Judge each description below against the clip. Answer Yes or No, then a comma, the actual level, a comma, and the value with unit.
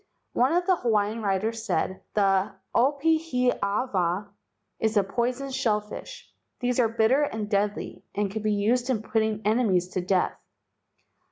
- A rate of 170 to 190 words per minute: No, average, 150 wpm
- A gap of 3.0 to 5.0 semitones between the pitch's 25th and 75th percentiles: Yes, average, 3.7 semitones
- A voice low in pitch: No, high, 220 Hz